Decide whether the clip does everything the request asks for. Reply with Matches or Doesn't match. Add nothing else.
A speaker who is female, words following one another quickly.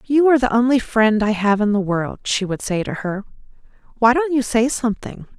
Matches